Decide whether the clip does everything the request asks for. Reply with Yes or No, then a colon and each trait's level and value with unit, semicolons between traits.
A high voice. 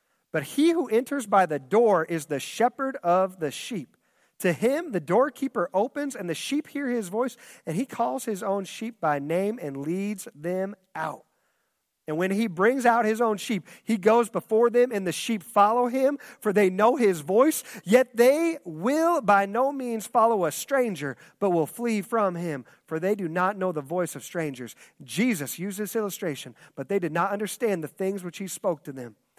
Yes: high, 205 Hz